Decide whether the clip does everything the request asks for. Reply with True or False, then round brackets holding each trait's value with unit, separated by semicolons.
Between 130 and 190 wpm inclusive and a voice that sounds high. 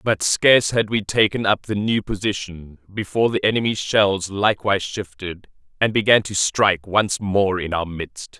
False (170 wpm; 100 Hz)